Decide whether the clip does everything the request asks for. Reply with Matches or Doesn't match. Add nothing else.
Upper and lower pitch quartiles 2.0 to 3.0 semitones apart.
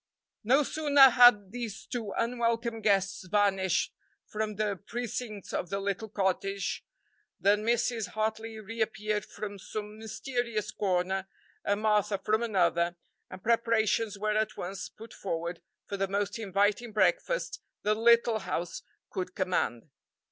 Matches